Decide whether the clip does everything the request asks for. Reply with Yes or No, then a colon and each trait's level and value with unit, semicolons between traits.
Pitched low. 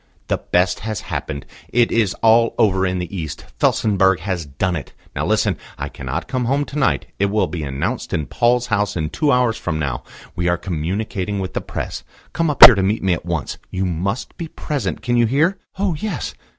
Yes: low, 100 Hz